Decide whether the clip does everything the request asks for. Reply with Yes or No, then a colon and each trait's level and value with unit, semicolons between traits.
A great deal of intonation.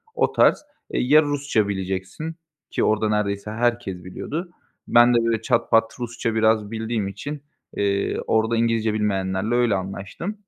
No: average, 3.0 semitones